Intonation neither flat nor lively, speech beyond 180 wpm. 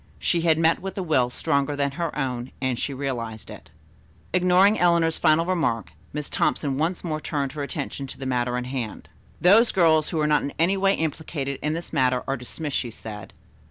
Yes: average, 4.2 semitones; average, 200 wpm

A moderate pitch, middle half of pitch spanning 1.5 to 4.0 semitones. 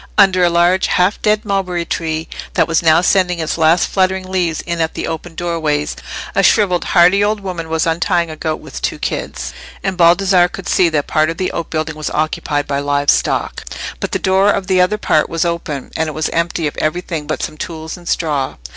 Yes: medium, 170 Hz; average, 2.7 semitones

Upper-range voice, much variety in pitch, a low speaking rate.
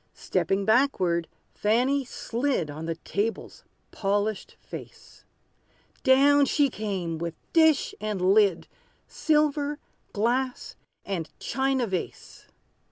Yes: high, 220 Hz; wide, 6.2 semitones; slow, 100 wpm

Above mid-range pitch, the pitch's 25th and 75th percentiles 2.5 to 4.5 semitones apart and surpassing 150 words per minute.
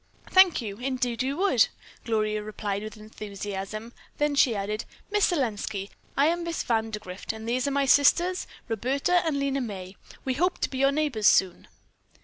No: high, 240 Hz; average, 4.9 semitones; average, 165 wpm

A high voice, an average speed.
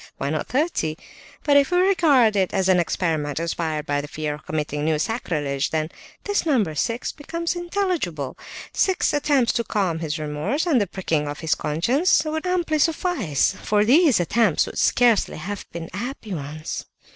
Yes: high, 195 Hz; average, 170 wpm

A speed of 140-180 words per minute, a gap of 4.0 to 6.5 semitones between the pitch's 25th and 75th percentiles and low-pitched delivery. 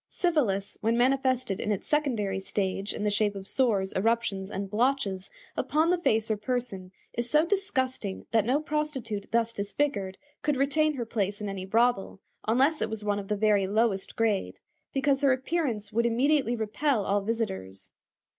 No: average, 170 wpm; average, 5.0 semitones; high, 225 Hz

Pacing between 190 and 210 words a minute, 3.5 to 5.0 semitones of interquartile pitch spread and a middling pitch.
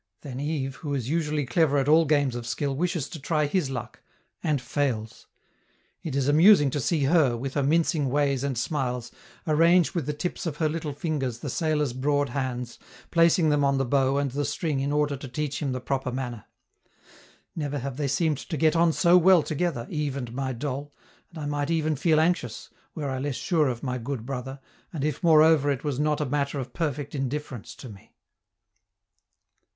No: average, 200 wpm; average, 2.8 semitones; medium, 145 Hz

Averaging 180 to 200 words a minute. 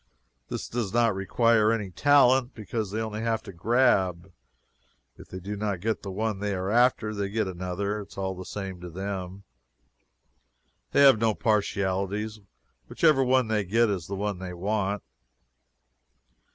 No: average, 165 wpm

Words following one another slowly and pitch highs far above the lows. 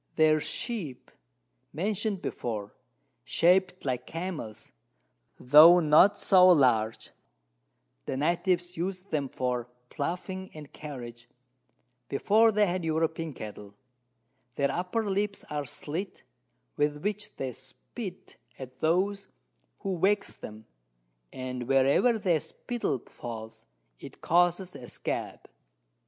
Yes: slow, 110 wpm; wide, 6.3 semitones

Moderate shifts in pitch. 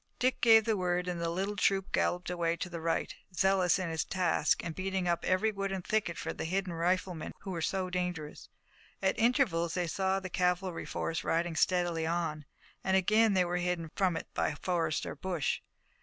No: narrow, 2.2 semitones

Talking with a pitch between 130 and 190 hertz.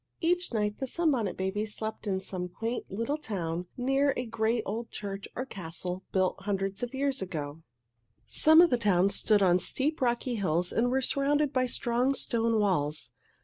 No: high, 220 Hz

